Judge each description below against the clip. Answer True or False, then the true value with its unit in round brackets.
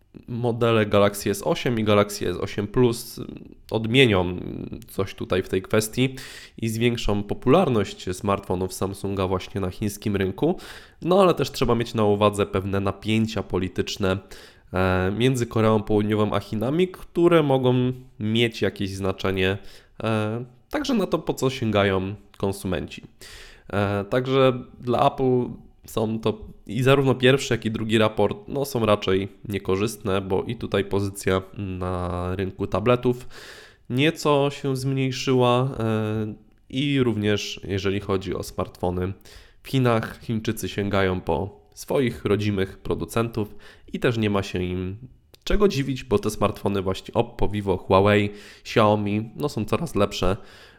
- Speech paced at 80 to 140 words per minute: True (130 wpm)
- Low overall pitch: True (105 Hz)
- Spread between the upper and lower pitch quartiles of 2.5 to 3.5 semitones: False (4.0 semitones)